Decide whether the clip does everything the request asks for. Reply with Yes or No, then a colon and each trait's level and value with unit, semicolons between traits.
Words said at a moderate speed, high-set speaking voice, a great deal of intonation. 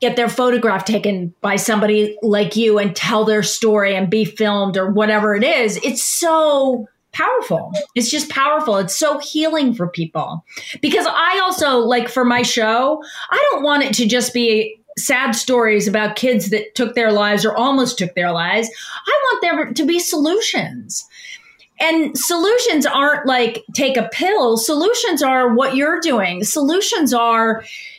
Yes: average, 165 wpm; high, 245 Hz; wide, 5.7 semitones